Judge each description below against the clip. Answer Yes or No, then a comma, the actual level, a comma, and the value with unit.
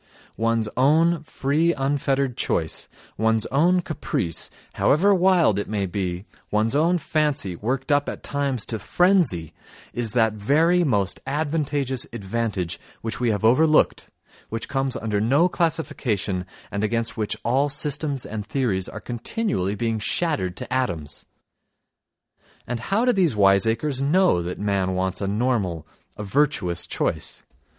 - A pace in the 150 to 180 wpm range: No, slow, 135 wpm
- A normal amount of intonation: No, wide, 6.4 semitones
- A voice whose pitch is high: No, low, 120 Hz